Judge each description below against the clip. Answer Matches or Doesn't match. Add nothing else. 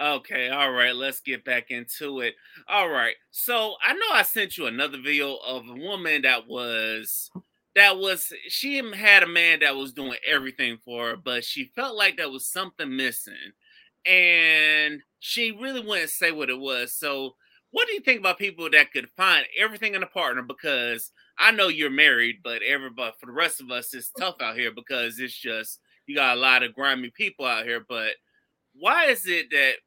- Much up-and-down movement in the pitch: Matches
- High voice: Doesn't match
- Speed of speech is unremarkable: Matches